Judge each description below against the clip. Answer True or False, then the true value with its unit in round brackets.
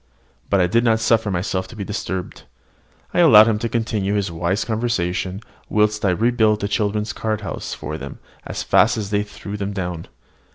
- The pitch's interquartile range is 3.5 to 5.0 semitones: False (2.5 semitones)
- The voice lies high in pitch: False (105 Hz)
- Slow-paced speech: False (190 wpm)